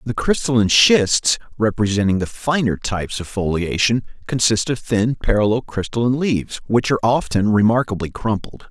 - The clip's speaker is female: No, male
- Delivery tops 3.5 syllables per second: Yes, 5.4 syllables/s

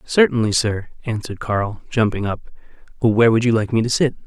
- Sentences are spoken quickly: No, average, 185 wpm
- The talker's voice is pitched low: Yes, low, 115 Hz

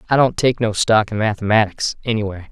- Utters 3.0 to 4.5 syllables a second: No, 5.9 syllables/s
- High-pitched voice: No, low, 110 Hz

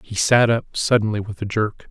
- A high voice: No, low, 105 Hz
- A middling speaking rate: No, fast, 220 wpm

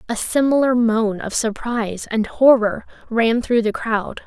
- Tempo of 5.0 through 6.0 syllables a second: No, 4.2 syllables/s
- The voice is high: Yes, high, 230 Hz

